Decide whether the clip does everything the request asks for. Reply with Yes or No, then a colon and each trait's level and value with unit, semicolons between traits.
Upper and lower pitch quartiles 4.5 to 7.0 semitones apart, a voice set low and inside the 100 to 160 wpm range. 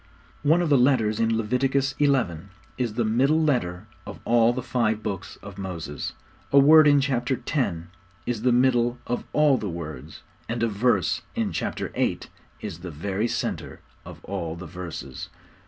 No: average, 5.3 semitones; low, 115 Hz; average, 170 wpm